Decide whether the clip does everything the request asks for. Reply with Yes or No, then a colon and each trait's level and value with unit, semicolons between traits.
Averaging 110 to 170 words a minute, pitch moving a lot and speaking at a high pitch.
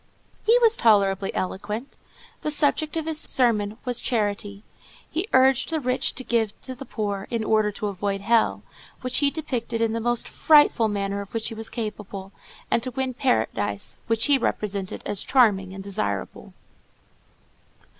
No: average, 165 wpm; average, 4.3 semitones; high, 225 Hz